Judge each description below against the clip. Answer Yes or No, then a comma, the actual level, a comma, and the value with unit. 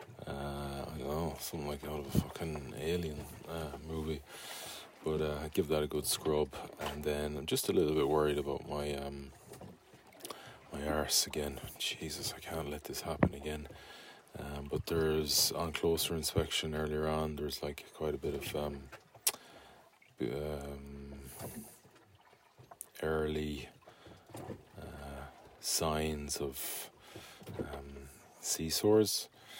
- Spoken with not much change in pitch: Yes, narrow, 1.6 semitones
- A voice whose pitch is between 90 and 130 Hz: No, very low, 75 Hz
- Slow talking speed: Yes, slow, 130 wpm